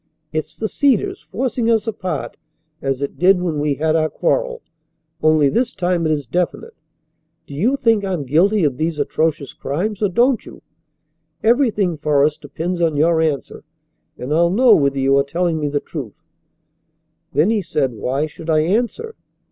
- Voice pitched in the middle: Yes, medium, 165 Hz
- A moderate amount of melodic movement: No, wide, 6.4 semitones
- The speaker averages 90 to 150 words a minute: No, average, 170 wpm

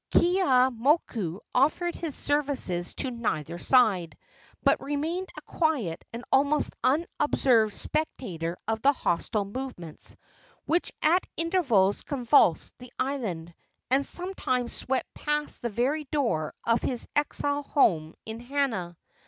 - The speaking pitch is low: No, very high, 255 Hz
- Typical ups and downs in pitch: No, wide, 6.3 semitones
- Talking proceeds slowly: Yes, slow, 120 wpm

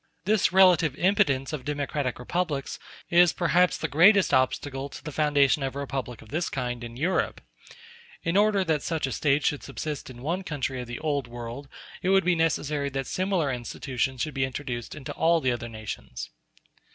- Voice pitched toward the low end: No, medium, 145 Hz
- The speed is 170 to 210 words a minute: Yes, average, 185 wpm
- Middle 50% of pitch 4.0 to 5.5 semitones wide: Yes, average, 4.3 semitones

